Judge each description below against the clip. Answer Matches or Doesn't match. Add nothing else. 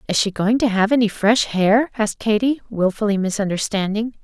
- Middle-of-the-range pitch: Doesn't match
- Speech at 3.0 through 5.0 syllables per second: Doesn't match